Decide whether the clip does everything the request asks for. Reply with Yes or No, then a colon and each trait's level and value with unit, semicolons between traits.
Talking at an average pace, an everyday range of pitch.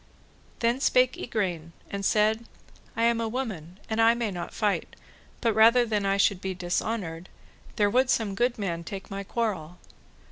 Yes: average, 170 wpm; average, 3.6 semitones